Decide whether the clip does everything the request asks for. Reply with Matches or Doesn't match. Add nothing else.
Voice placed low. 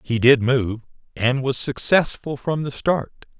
Matches